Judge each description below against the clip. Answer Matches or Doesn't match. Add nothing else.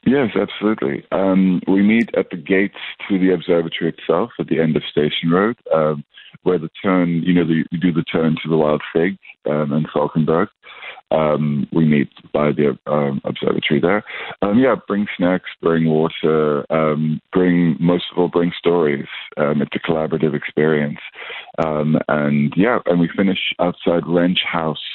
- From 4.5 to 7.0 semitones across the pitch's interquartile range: Doesn't match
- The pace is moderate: Matches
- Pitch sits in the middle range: Doesn't match